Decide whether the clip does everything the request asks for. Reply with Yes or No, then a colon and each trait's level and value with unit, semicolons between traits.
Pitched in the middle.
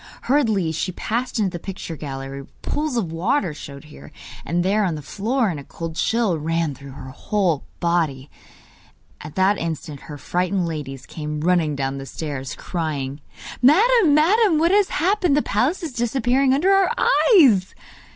Yes: medium, 180 Hz